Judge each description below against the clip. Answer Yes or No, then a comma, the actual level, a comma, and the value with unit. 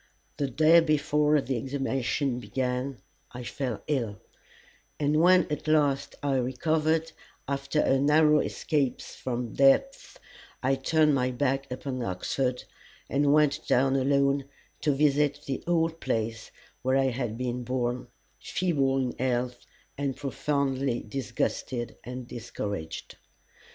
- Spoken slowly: Yes, slow, 125 wpm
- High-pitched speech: No, low, 135 Hz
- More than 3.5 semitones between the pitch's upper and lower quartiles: No, average, 2.8 semitones